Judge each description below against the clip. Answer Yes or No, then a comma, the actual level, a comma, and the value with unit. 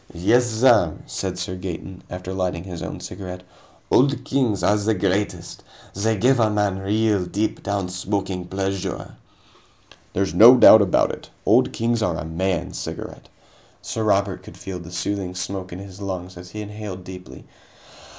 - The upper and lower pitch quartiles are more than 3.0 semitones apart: No, average, 2.7 semitones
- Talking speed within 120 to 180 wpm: Yes, average, 160 wpm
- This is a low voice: Yes, very low, 95 Hz